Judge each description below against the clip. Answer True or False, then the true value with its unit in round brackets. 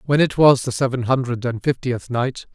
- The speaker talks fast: True (215 wpm)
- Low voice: True (125 Hz)